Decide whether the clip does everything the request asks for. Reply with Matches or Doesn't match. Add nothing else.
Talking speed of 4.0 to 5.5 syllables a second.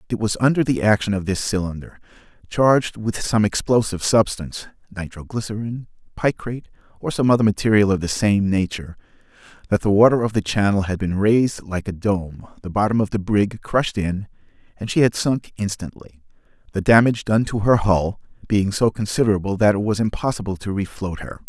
Doesn't match